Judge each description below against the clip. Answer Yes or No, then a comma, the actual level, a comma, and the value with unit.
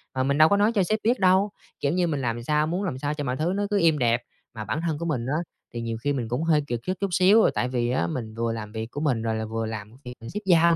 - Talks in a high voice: No, medium, 145 Hz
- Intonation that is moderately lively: No, wide, 6.6 semitones